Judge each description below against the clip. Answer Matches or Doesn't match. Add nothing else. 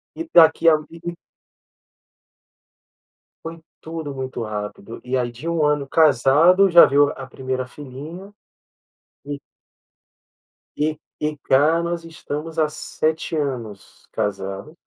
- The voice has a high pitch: Doesn't match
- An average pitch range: Matches